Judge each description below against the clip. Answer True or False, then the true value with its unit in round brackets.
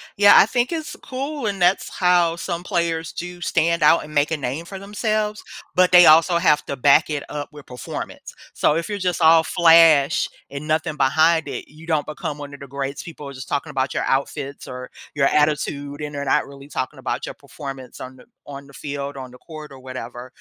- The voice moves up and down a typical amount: True (3.6 semitones)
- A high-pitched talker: False (150 Hz)